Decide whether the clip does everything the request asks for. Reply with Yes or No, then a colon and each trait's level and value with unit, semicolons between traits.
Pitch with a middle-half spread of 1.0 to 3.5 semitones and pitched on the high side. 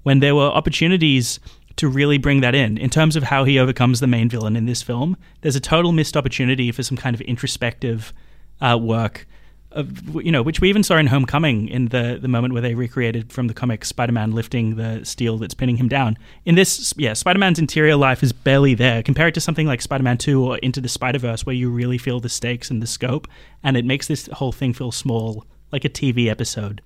No: average, 3.2 semitones; low, 130 Hz